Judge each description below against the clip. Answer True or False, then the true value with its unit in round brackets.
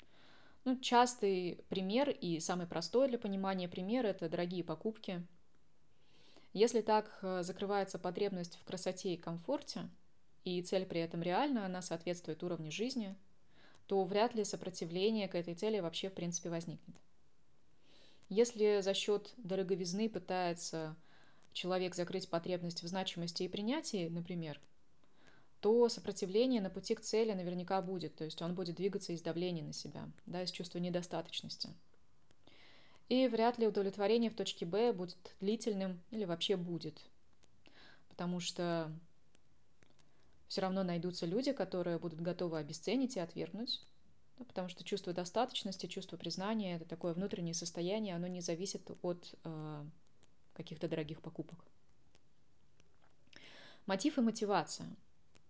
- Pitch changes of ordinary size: True (3.4 semitones)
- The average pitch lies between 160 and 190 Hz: True (185 Hz)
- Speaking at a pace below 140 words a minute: True (130 wpm)